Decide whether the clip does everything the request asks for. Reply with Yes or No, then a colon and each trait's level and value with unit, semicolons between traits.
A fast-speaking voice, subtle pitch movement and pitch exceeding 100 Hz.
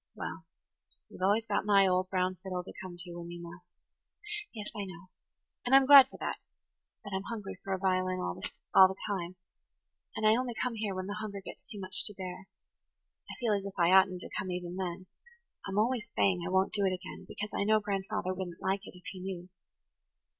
Yes: fast, 210 wpm; narrow, 2.2 semitones; high, 190 Hz